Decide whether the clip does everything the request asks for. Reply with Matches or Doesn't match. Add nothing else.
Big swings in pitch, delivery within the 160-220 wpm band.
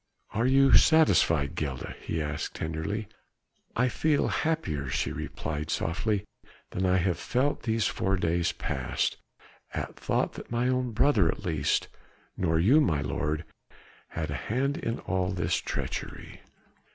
Doesn't match